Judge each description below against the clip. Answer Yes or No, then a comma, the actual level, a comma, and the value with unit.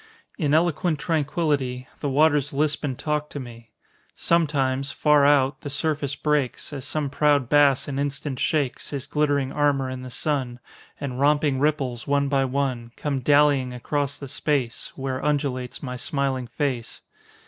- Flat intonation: Yes, narrow, 2.1 semitones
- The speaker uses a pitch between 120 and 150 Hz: Yes, medium, 140 Hz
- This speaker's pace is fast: No, average, 155 wpm